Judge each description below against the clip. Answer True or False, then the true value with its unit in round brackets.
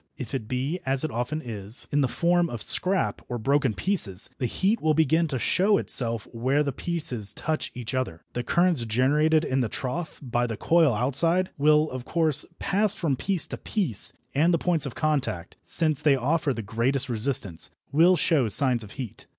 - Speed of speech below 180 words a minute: False (190 wpm)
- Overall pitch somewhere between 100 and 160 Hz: True (140 Hz)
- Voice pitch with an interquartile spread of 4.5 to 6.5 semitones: True (5.0 semitones)